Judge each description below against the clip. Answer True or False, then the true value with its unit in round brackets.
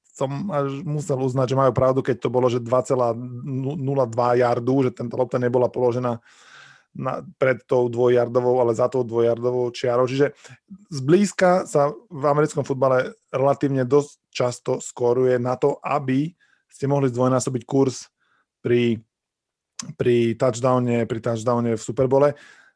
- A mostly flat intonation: True (2.3 semitones)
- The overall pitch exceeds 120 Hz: True (130 Hz)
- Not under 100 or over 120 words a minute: False (135 wpm)